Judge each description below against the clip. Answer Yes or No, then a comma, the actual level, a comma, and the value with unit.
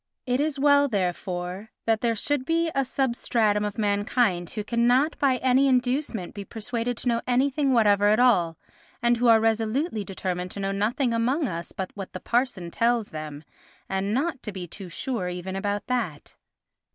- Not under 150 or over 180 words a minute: Yes, average, 175 wpm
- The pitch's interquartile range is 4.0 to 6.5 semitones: Yes, average, 4.5 semitones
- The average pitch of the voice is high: Yes, high, 225 Hz